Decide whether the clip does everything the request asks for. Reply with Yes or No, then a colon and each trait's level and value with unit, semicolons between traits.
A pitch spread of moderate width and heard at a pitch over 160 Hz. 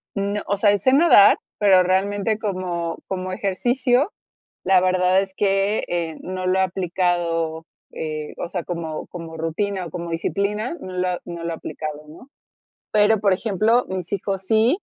Yes: average, 3.0 semitones; medium, 185 Hz